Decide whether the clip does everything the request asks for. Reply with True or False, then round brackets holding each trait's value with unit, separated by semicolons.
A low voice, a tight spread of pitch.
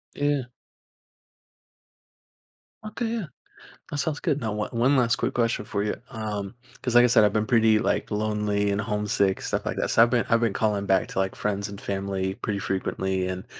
False (105 Hz; 3.0 semitones)